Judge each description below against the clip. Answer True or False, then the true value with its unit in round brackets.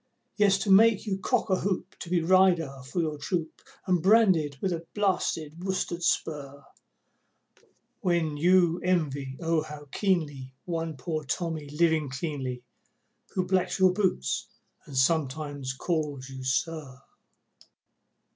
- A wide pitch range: False (4.2 semitones)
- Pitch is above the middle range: False (165 Hz)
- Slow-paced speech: True (130 wpm)